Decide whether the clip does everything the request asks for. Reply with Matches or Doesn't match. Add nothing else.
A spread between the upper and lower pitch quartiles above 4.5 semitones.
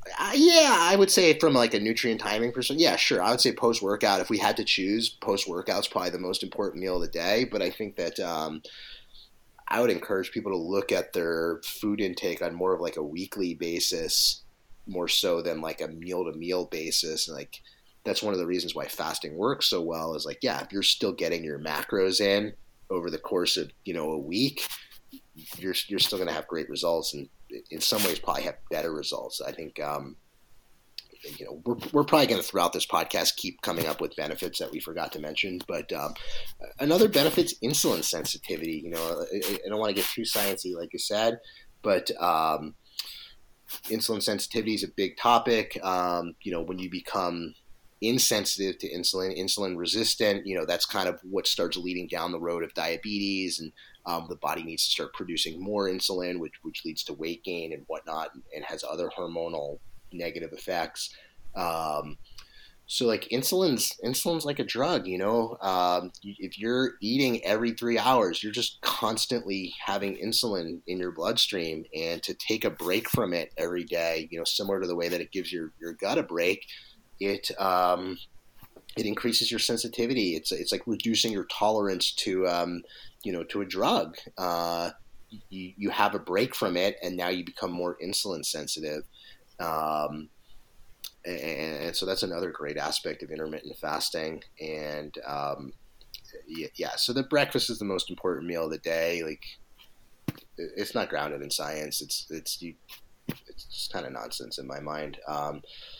Matches